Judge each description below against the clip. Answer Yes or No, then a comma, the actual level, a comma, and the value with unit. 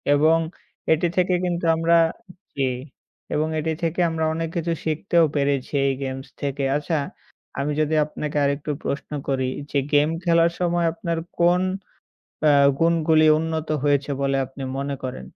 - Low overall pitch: No, medium, 155 Hz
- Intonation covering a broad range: No, average, 2.8 semitones